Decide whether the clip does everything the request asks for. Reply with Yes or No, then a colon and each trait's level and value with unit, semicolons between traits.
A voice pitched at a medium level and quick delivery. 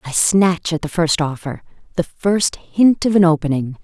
No: medium, 170 Hz; average, 190 wpm